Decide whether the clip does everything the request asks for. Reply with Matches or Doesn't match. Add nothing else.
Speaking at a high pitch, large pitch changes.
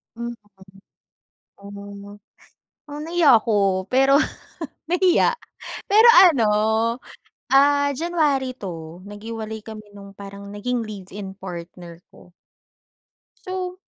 Matches